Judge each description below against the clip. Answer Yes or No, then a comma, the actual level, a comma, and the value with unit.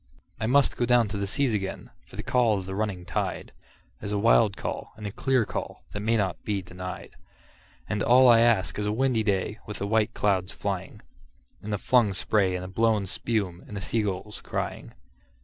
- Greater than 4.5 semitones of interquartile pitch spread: No, average, 2.8 semitones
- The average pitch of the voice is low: Yes, low, 105 Hz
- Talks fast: Yes, fast, 210 wpm